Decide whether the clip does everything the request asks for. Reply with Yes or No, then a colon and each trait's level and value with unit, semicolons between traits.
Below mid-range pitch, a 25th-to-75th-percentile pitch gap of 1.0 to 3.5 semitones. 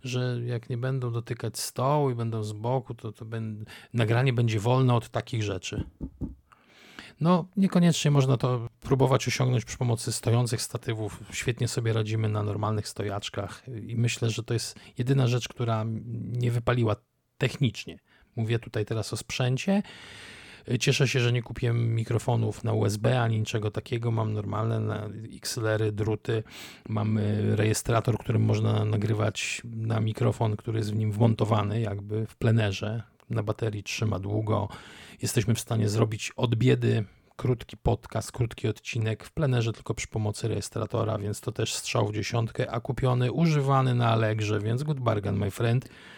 Yes: low, 115 Hz; narrow, 2.4 semitones